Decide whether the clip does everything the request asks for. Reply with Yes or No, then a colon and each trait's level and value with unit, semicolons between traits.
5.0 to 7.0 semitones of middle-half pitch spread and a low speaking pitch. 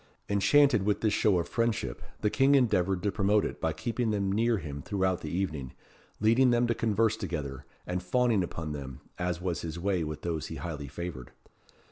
Yes: wide, 5.4 semitones; very low, 95 Hz